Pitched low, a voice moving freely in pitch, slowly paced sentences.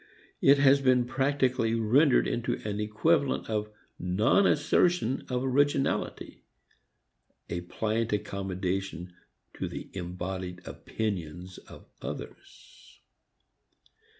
Yes: low, 110 Hz; wide, 6.2 semitones; slow, 95 wpm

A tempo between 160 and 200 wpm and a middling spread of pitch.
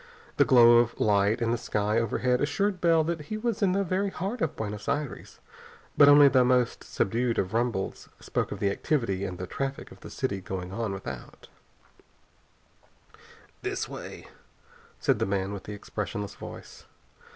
No: average, 170 wpm; wide, 6.5 semitones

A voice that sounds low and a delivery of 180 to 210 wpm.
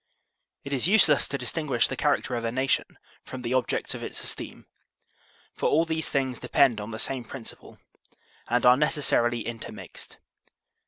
No: low, 130 Hz; average, 170 wpm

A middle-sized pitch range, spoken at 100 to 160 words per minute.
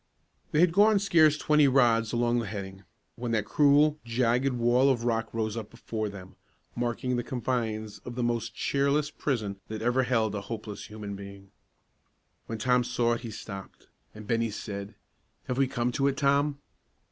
No: average, 3.8 semitones; average, 175 wpm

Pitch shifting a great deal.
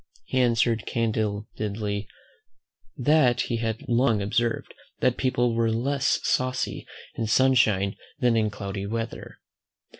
No: narrow, 2.6 semitones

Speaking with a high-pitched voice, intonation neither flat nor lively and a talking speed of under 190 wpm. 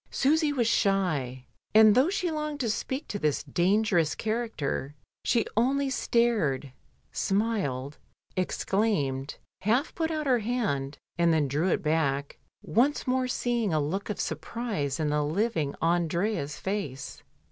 No: high, 200 Hz; wide, 8.2 semitones; slow, 135 wpm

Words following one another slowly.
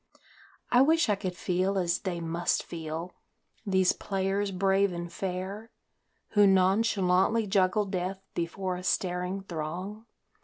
Yes: slow, 125 wpm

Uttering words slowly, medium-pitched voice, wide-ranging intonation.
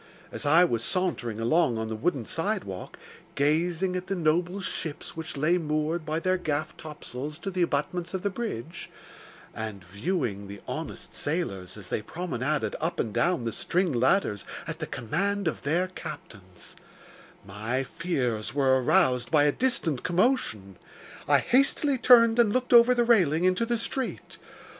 No: average, 160 wpm; medium, 160 Hz; wide, 7.2 semitones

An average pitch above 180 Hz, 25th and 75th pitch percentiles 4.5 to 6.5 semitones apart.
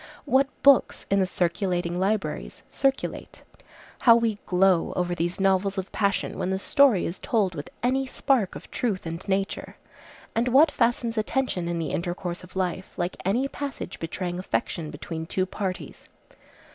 Yes: high, 190 Hz; average, 4.8 semitones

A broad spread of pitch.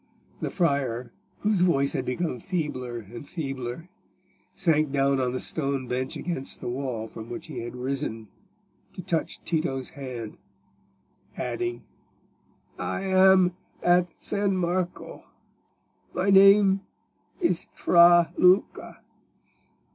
Yes: wide, 6.1 semitones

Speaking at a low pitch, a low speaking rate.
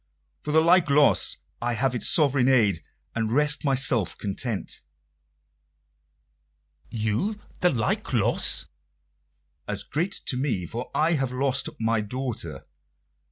Yes: low, 130 Hz; slow, 120 wpm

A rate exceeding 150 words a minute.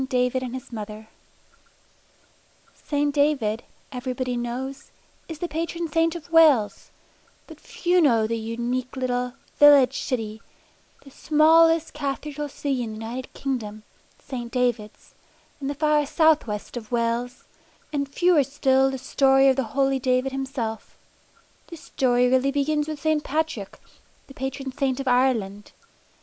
No: average, 140 wpm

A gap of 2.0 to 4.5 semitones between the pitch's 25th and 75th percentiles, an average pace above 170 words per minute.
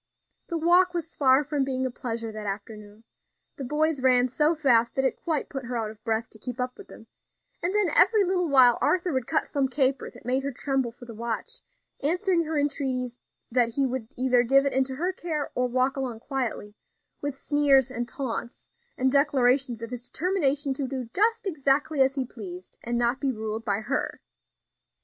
Yes: average, 3.5 semitones; average, 200 wpm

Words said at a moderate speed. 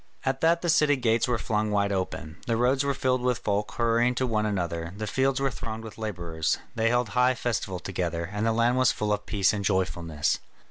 No: fast, 220 wpm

